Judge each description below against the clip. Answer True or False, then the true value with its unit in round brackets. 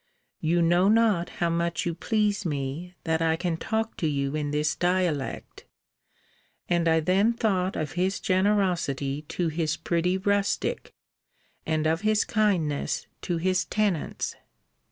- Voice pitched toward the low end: False (175 Hz)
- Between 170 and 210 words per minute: False (140 wpm)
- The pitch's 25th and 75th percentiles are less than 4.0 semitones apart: True (3.5 semitones)